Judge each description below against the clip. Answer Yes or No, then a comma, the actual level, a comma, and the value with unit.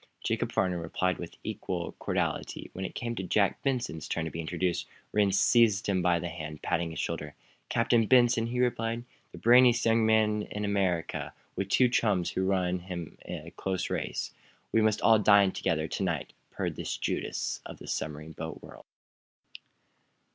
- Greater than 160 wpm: Yes, average, 170 wpm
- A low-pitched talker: Yes, very low, 95 Hz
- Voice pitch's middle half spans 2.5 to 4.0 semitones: No, average, 4.6 semitones